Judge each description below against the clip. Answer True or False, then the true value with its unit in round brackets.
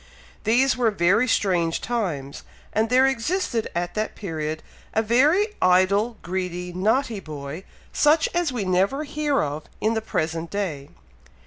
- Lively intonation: True (6.3 semitones)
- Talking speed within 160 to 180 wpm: False (140 wpm)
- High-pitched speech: True (205 Hz)